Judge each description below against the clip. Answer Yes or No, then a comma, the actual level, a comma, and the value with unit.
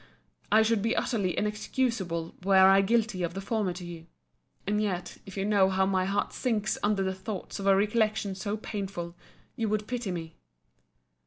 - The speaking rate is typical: Yes, average, 180 wpm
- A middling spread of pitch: No, narrow, 2.2 semitones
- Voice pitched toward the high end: Yes, high, 195 Hz